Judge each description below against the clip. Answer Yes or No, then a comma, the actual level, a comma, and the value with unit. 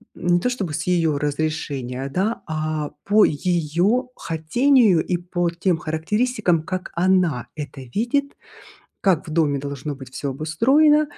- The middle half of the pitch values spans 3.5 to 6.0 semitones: Yes, average, 5.1 semitones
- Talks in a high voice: No, medium, 170 Hz